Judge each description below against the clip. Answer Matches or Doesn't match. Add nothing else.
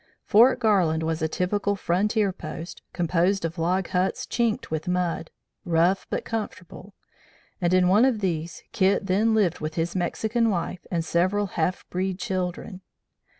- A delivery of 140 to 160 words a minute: Matches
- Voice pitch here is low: Doesn't match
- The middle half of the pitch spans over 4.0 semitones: Doesn't match